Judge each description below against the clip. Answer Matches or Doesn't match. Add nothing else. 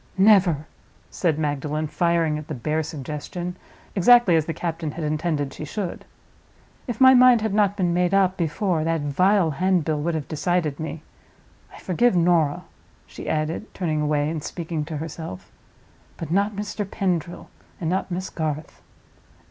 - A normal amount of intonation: Matches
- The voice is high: Doesn't match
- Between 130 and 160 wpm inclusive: Matches